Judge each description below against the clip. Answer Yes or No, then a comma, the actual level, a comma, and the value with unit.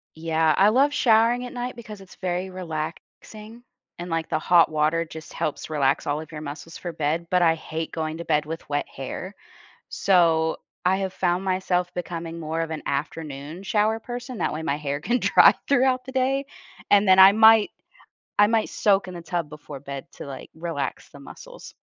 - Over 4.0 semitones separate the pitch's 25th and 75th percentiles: Yes, average, 4.9 semitones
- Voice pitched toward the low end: No, medium, 170 Hz